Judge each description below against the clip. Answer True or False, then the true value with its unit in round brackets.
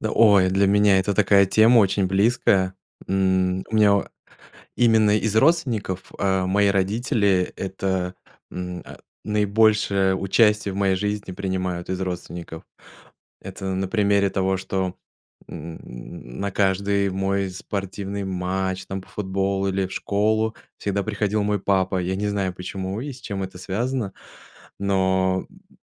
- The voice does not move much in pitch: True (1.6 semitones)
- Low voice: True (95 Hz)